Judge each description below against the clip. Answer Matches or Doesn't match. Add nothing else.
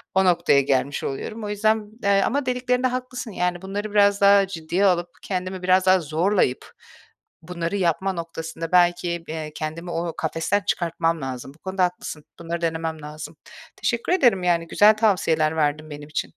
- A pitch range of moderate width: Matches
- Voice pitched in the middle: Matches